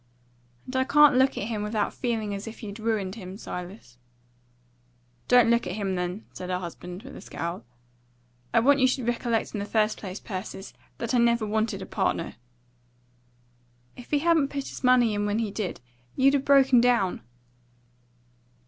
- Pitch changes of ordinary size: Yes, average, 4.1 semitones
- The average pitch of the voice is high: Yes, high, 225 Hz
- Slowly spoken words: No, average, 175 wpm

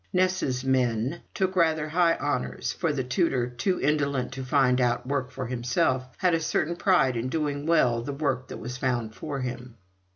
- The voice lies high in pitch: No, low, 135 Hz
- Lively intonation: No, average, 4.1 semitones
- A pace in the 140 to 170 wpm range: No, average, 185 wpm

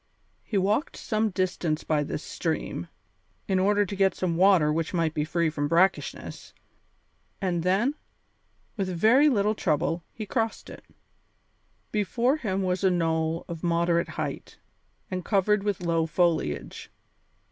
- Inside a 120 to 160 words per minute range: Yes, average, 140 wpm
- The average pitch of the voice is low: No, medium, 180 Hz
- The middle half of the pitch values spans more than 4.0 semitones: No, average, 3.6 semitones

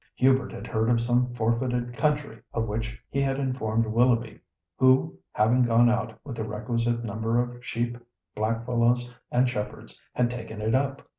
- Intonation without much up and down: Yes, narrow, 1.8 semitones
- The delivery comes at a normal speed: Yes, average, 160 wpm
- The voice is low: Yes, low, 120 Hz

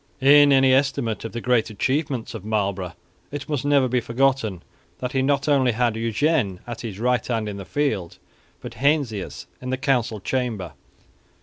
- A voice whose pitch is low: Yes, low, 125 Hz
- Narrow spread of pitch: No, average, 3.9 semitones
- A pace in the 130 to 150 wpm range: No, average, 175 wpm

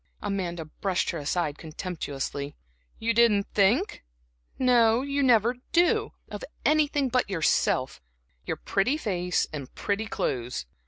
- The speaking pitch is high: Yes, high, 200 Hz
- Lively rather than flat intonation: Yes, wide, 7.1 semitones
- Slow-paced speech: Yes, slow, 120 wpm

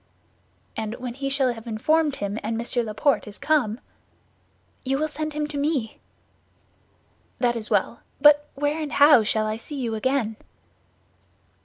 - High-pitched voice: Yes, very high, 260 Hz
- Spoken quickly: No, average, 155 wpm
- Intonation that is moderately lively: Yes, average, 4.8 semitones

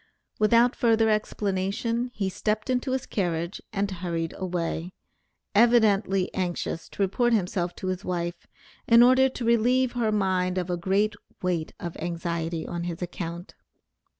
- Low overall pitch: No, high, 190 Hz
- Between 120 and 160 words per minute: Yes, average, 145 wpm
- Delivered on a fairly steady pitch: No, average, 4.4 semitones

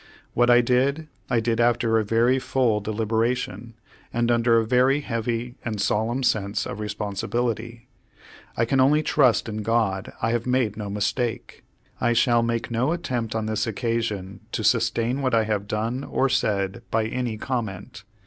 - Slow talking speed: No, average, 165 wpm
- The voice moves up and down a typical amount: No, narrow, 2.2 semitones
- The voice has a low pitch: Yes, low, 115 Hz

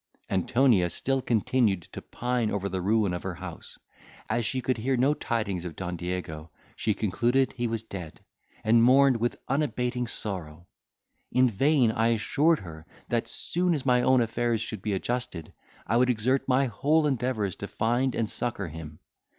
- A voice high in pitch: No, low, 115 Hz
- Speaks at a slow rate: No, average, 170 wpm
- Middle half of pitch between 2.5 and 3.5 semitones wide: No, average, 4.9 semitones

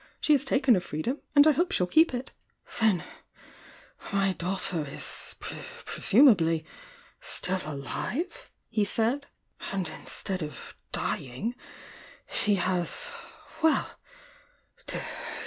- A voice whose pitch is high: Yes, high, 200 Hz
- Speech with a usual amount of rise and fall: No, wide, 7.3 semitones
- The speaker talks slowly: Yes, slow, 115 wpm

